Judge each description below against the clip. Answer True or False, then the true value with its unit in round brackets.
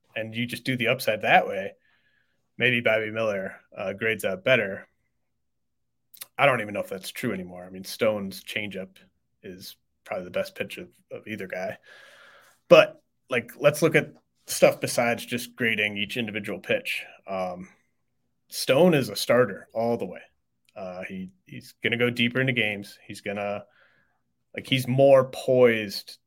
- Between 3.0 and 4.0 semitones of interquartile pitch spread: True (3.6 semitones)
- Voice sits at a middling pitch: False (110 Hz)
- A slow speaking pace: False (165 wpm)